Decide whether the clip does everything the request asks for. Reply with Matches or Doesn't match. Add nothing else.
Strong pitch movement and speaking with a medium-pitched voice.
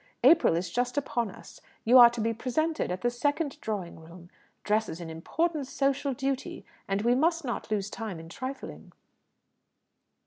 Doesn't match